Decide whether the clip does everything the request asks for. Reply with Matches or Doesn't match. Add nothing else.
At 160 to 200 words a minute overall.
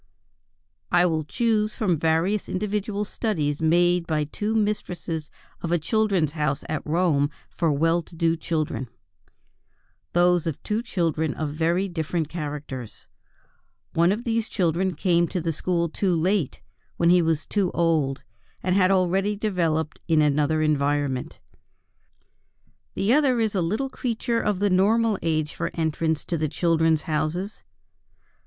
Doesn't match